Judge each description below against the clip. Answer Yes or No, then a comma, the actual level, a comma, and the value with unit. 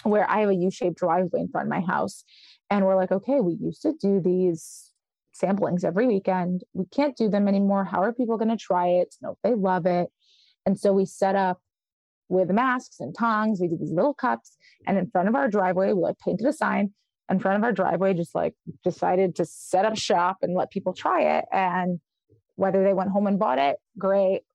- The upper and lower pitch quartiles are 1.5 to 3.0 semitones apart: Yes, average, 2.7 semitones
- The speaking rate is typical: No, fast, 220 wpm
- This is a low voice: No, high, 195 Hz